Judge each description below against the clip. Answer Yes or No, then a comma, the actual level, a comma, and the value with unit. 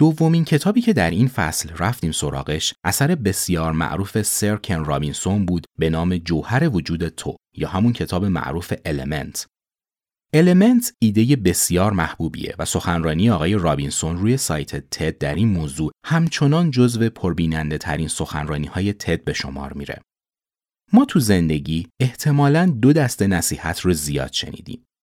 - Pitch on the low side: Yes, very low, 90 Hz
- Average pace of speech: Yes, average, 140 wpm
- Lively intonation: Yes, wide, 7.5 semitones